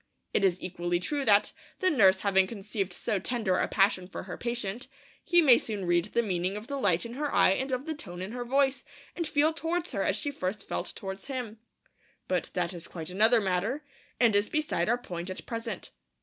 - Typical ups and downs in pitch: No, wide, 5.7 semitones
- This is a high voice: Yes, high, 210 Hz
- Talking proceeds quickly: Yes, fast, 215 wpm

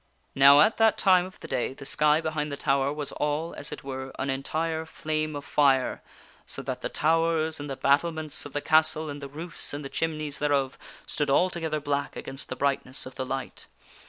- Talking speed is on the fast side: Yes, fast, 215 wpm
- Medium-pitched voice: Yes, medium, 150 Hz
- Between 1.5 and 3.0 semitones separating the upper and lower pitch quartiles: Yes, narrow, 2.4 semitones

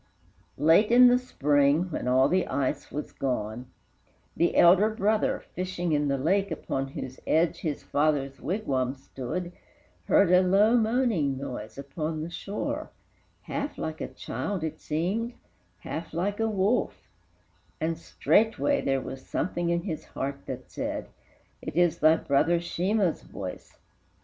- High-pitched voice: No, medium, 165 Hz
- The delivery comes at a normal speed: Yes, average, 145 wpm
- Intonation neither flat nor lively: No, wide, 5.9 semitones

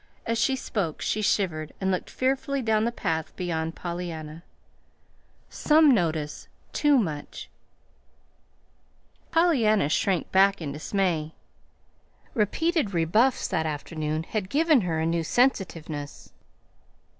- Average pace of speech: No, slow, 110 wpm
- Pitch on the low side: No, medium, 185 Hz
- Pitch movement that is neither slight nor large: No, wide, 6.7 semitones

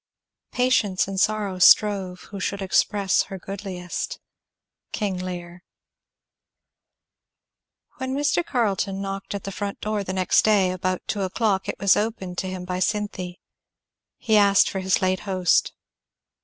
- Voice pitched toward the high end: Yes, high, 195 Hz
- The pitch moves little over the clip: Yes, narrow, 2.0 semitones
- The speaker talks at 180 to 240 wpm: No, average, 140 wpm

